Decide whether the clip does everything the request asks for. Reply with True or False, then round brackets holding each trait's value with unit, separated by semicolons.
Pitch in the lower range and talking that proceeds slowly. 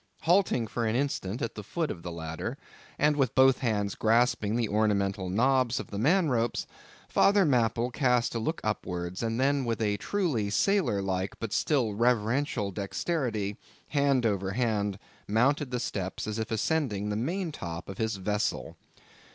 False (115 Hz; 170 wpm)